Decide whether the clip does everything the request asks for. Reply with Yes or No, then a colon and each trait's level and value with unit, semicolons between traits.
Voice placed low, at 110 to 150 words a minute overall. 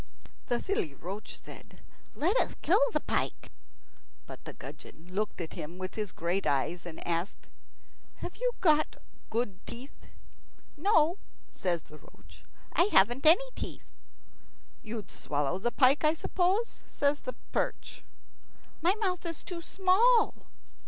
No: very high, 255 Hz; average, 140 wpm